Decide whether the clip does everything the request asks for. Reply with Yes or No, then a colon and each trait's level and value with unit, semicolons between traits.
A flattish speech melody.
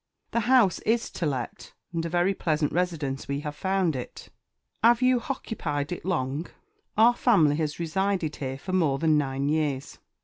No: average, 5.0 semitones